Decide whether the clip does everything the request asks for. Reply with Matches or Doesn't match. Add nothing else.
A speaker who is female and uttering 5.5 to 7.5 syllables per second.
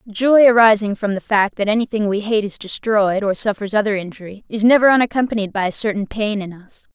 Matches